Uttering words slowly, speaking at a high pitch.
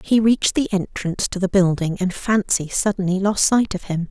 No: fast, 205 wpm; high, 195 Hz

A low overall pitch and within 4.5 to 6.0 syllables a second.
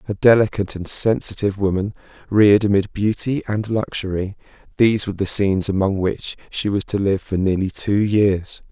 Yes: low, 100 Hz; 5.5 syllables/s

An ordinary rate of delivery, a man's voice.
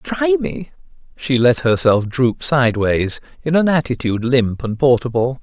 Yes: average, 145 wpm; male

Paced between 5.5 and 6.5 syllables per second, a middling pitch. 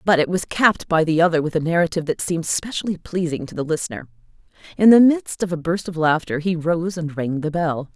Yes: 6.0 syllables/s; medium, 170 Hz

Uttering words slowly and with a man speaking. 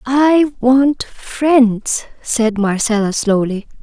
No: slow, 95 wpm; female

